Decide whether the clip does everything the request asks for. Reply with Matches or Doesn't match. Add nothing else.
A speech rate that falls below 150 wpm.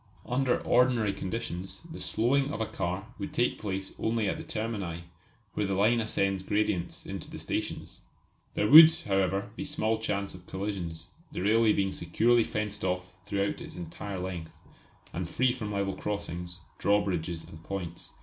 Doesn't match